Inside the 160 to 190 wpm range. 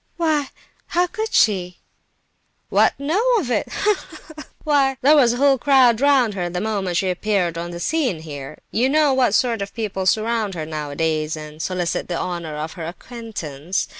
Yes: average, 185 wpm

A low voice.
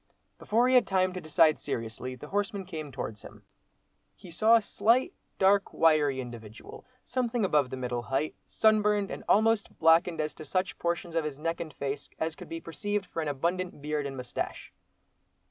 No: medium, 165 Hz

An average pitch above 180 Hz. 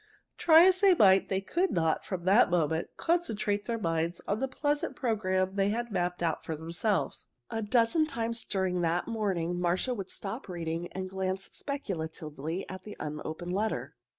Yes: high, 190 Hz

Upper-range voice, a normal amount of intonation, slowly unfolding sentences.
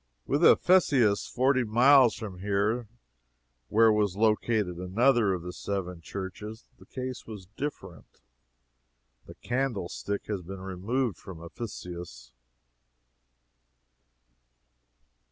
No: low, 105 Hz; average, 4.5 semitones; slow, 100 wpm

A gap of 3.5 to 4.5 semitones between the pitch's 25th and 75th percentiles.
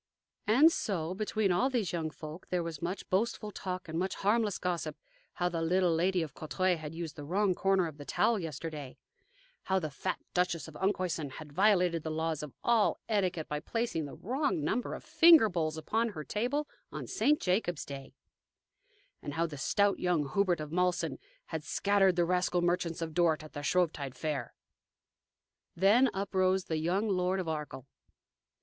Yes: average, 3.8 semitones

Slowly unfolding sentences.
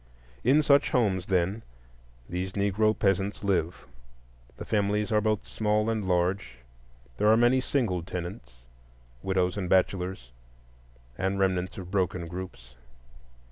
Yes: slow, 120 wpm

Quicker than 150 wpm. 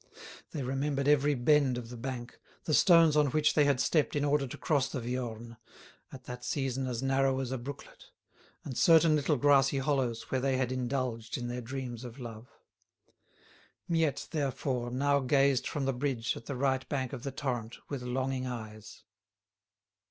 Yes: average, 175 wpm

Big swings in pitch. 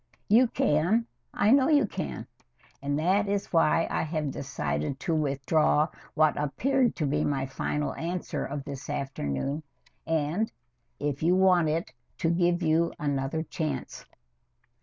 No: average, 4.1 semitones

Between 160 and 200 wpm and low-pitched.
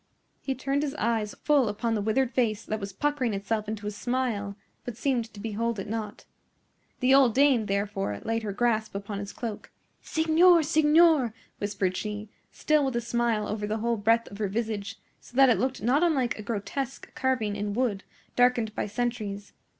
No: average, 185 wpm; high, 225 Hz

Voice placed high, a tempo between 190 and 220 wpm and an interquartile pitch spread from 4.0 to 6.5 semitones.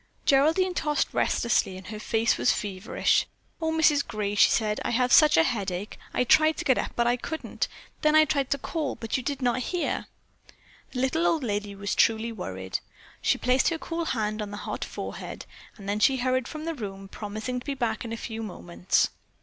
Yes: high, 240 Hz; fast, 205 wpm; wide, 5.4 semitones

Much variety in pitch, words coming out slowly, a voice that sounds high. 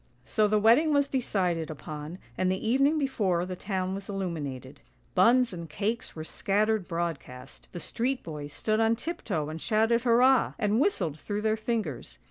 No: wide, 5.8 semitones; average, 170 wpm; high, 200 Hz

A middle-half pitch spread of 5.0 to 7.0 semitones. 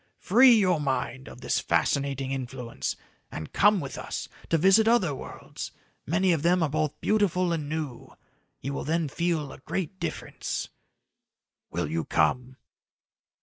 Yes: average, 5.3 semitones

